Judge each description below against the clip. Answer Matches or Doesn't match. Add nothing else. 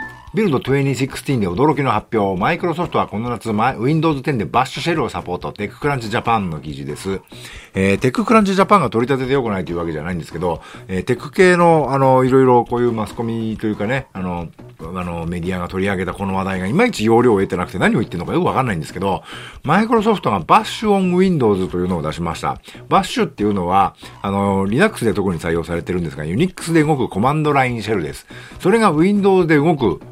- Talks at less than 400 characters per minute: Doesn't match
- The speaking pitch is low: Matches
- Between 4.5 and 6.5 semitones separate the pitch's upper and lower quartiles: Doesn't match